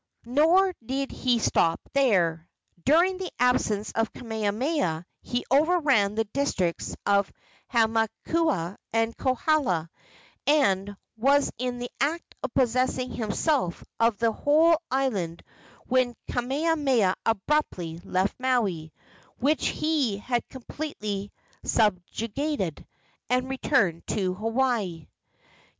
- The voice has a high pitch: Yes, high, 240 Hz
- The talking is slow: Yes, slow, 100 wpm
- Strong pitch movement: Yes, wide, 5.7 semitones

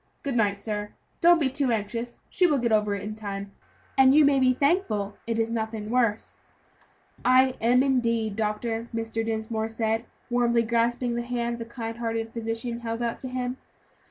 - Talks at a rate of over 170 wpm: Yes, average, 180 wpm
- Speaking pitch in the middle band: No, high, 230 Hz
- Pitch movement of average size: No, narrow, 2.0 semitones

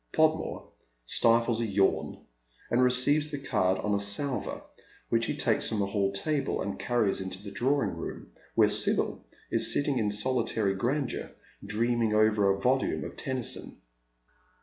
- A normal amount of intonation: Yes, average, 4.4 semitones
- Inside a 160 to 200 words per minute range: No, average, 150 wpm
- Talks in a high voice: No, low, 115 Hz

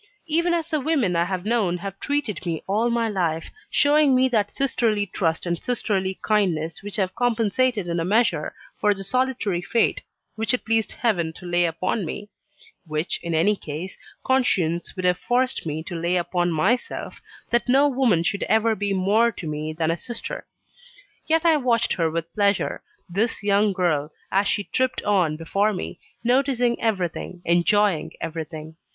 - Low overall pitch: No, high, 200 Hz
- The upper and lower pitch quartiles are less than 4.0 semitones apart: No, wide, 5.5 semitones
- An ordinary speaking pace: Yes, average, 170 wpm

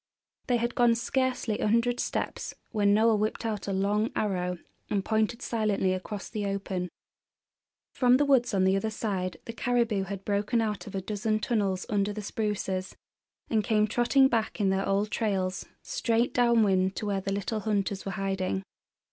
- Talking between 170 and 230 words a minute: Yes, average, 175 wpm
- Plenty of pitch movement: No, average, 2.8 semitones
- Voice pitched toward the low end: No, high, 210 Hz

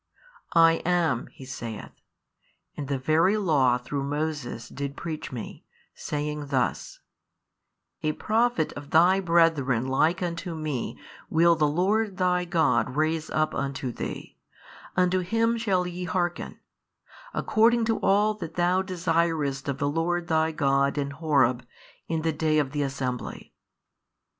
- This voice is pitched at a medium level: Yes, medium, 160 Hz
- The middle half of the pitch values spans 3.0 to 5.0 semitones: Yes, average, 4.1 semitones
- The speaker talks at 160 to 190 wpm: No, average, 140 wpm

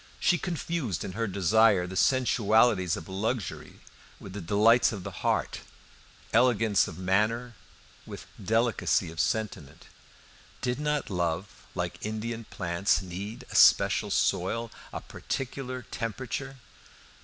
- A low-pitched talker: Yes, low, 110 Hz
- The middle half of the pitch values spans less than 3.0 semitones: No, average, 4.5 semitones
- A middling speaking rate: No, slow, 120 wpm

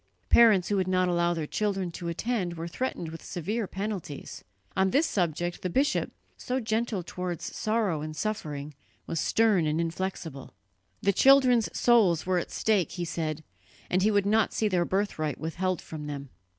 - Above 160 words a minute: Yes, average, 170 wpm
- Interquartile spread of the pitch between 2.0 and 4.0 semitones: No, average, 4.5 semitones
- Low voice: No, medium, 185 Hz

